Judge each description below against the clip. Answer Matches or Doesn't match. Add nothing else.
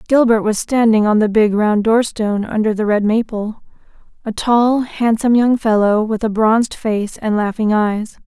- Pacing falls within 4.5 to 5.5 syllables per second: Matches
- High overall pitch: Matches